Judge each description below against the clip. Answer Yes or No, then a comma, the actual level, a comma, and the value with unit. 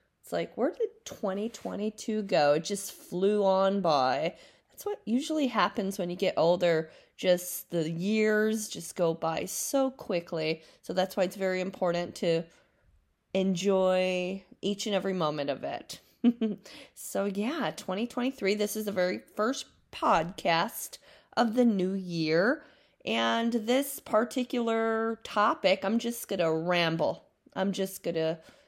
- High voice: Yes, high, 195 Hz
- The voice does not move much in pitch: No, average, 4.3 semitones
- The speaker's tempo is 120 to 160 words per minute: Yes, average, 140 wpm